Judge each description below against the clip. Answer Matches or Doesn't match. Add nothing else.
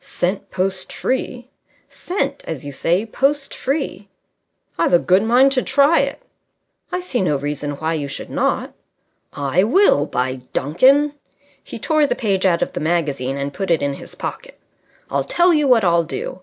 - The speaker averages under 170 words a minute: Doesn't match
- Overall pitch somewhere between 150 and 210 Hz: Matches